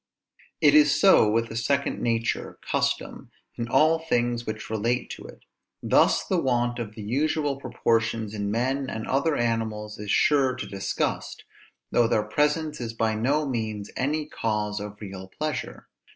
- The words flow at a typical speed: Yes, average, 160 wpm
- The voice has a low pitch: Yes, low, 120 Hz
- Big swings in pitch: No, average, 4.4 semitones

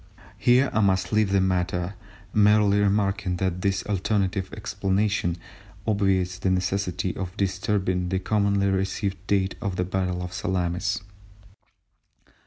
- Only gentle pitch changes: Yes, narrow, 1.7 semitones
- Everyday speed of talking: No, slow, 125 wpm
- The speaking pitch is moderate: No, very low, 95 Hz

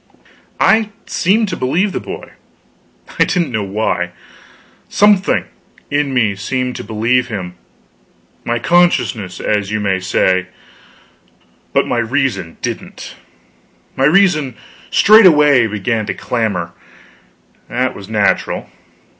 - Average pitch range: No, wide, 6.5 semitones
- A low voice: Yes, low, 120 Hz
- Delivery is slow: Yes, slow, 115 wpm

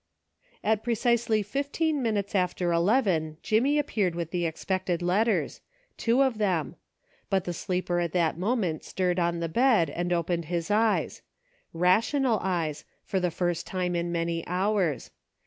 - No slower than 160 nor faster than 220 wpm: No, average, 150 wpm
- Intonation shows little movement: No, average, 4.4 semitones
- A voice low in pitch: No, medium, 185 Hz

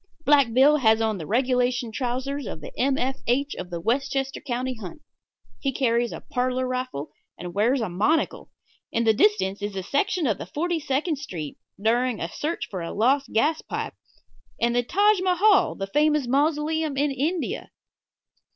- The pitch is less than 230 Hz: No, very high, 255 Hz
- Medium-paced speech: Yes, average, 170 wpm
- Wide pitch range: No, average, 4.7 semitones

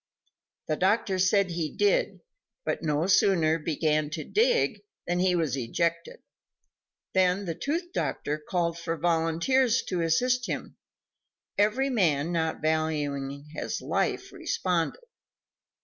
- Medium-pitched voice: Yes, medium, 170 Hz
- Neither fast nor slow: No, slow, 120 wpm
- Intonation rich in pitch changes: No, average, 4.6 semitones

